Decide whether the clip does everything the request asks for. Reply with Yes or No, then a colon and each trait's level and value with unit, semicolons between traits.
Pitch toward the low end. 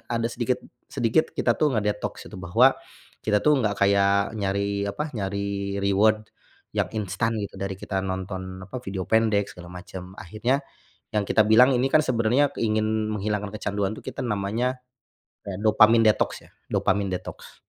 Yes: low, 105 Hz